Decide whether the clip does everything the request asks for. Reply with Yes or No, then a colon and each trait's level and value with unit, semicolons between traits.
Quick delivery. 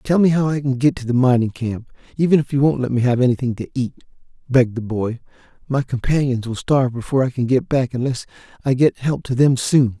Yes: fast, 235 wpm